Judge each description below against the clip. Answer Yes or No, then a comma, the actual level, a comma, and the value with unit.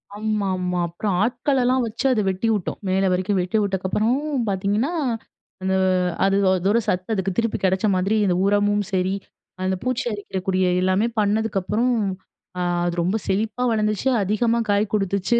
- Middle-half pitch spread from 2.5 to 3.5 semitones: Yes, average, 2.9 semitones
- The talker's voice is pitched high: Yes, high, 205 Hz